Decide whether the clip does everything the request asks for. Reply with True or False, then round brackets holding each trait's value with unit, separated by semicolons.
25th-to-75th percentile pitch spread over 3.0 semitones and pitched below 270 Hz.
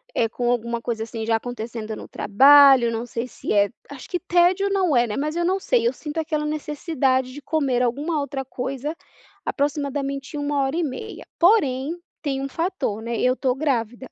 False (4.1 semitones; 275 Hz)